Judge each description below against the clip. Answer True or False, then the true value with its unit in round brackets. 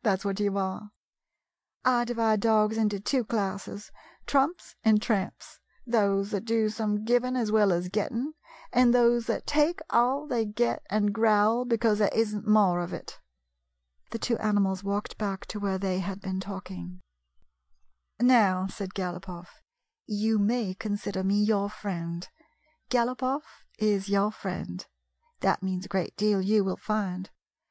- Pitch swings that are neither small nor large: True (3.3 semitones)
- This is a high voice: True (210 Hz)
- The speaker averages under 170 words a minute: True (150 wpm)